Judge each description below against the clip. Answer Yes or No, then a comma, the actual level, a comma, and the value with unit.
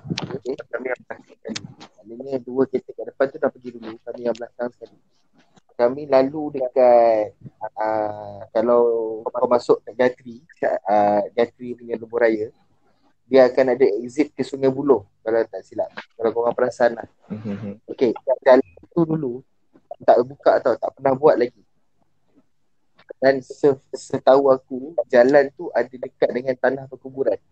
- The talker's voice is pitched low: Yes, low, 125 Hz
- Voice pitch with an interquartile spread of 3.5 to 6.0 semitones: No, average, 2.7 semitones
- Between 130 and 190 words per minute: Yes, average, 145 wpm